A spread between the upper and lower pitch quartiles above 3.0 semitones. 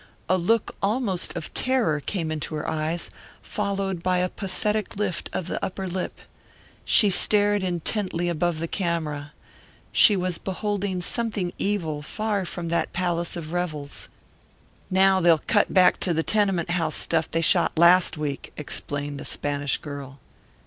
Yes: average, 3.7 semitones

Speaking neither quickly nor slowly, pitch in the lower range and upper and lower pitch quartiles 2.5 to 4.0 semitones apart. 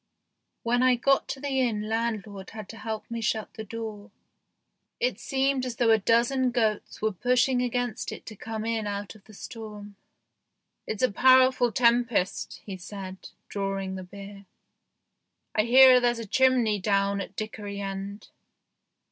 No: average, 165 wpm; high, 220 Hz; average, 3.3 semitones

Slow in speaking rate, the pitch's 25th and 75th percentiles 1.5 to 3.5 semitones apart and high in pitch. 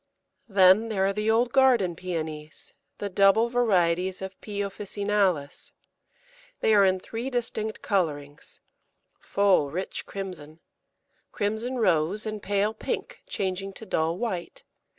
Yes: slow, 125 wpm; average, 3.2 semitones; high, 195 Hz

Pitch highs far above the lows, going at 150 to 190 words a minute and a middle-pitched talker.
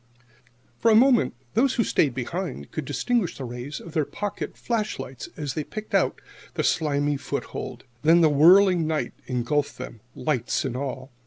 Yes: wide, 6.3 semitones; average, 170 wpm; medium, 150 Hz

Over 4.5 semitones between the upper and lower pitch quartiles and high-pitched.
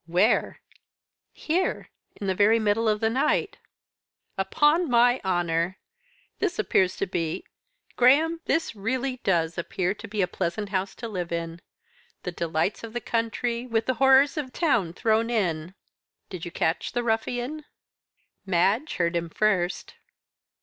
Yes: wide, 5.4 semitones; high, 215 Hz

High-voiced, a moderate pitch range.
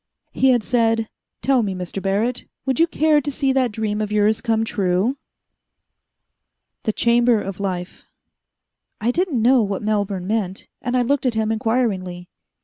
Yes: high, 225 Hz; average, 3.7 semitones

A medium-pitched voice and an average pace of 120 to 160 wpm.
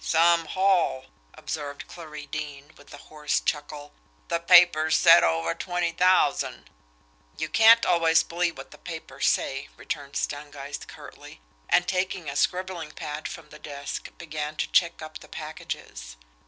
Yes: medium, 155 Hz; average, 145 wpm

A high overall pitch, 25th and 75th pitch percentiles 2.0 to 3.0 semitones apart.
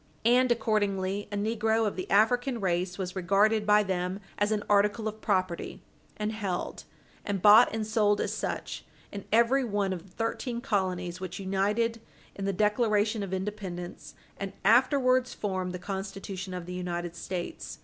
Yes: high, 205 Hz; average, 2.7 semitones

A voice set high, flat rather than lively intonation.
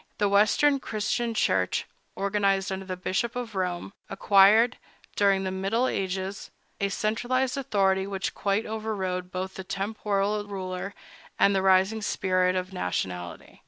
Yes: high, 195 Hz; narrow, 2.1 semitones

